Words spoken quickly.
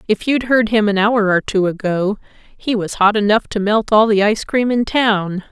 Yes: fast, 230 wpm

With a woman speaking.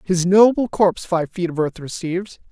No: male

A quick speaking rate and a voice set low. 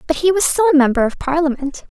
No: fast, 245 wpm; very high, 305 Hz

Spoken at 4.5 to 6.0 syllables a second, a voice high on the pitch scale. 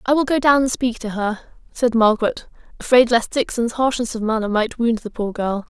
Yes: 5.3 syllables/s; high, 240 Hz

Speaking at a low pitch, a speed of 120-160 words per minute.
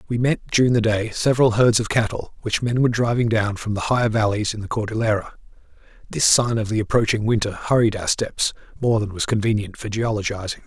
No: low, 110 Hz; fast, 205 wpm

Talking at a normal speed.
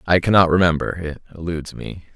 Yes: average, 165 wpm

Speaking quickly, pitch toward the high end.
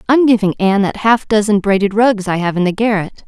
Yes: fast, 240 wpm; high, 205 Hz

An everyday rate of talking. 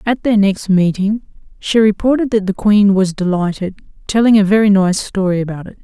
Yes: average, 185 wpm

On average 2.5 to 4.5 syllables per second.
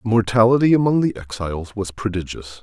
No: 5.9 syllables/s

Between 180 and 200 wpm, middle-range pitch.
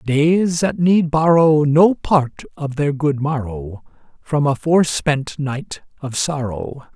No: average, 145 wpm; medium, 145 Hz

